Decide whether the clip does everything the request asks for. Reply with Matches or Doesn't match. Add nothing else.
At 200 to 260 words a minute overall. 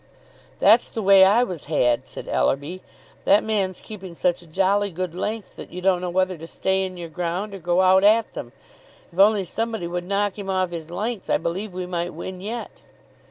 Matches